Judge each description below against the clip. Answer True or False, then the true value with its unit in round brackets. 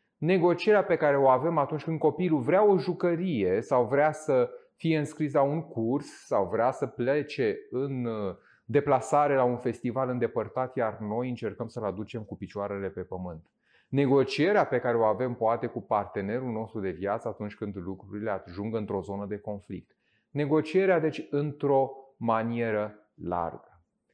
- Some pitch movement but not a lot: False (5.9 semitones)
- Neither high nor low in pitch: False (125 Hz)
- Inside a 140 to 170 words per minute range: True (155 wpm)